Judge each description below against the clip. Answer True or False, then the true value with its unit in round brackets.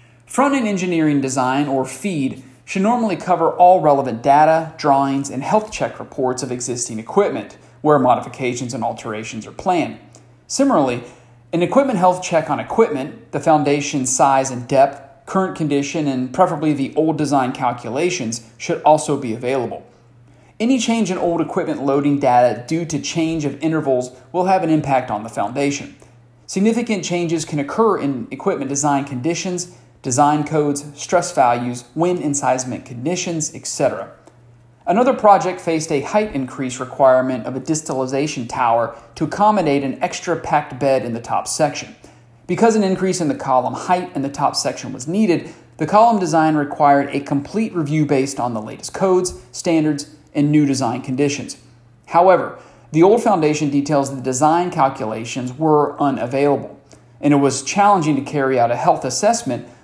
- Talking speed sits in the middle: True (155 wpm)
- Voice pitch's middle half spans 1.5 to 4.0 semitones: False (4.5 semitones)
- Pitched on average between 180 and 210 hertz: False (145 Hz)